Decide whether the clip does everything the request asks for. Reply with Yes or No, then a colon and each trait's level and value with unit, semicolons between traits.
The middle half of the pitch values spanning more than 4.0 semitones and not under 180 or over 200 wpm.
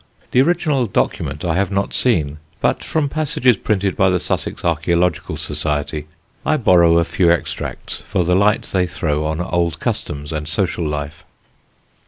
No: average, 4.7 semitones; average, 160 wpm